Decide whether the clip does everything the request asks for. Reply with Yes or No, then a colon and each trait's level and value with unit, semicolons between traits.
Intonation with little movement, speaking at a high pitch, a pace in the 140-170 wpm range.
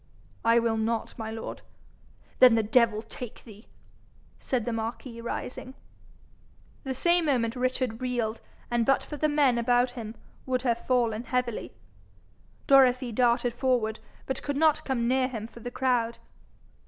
Yes: narrow, 2.2 semitones; high, 245 Hz; average, 150 wpm